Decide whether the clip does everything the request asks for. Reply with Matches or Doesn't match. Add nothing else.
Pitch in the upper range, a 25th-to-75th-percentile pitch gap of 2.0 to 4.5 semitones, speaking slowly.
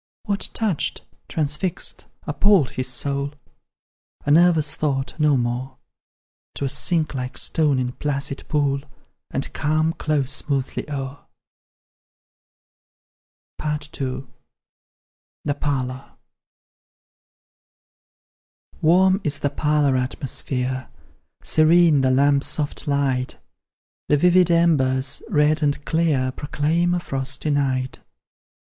Doesn't match